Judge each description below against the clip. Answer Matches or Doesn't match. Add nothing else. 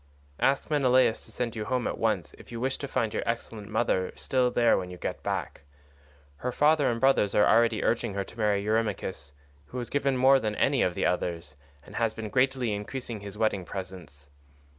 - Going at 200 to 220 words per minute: Matches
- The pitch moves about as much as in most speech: Matches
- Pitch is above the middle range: Doesn't match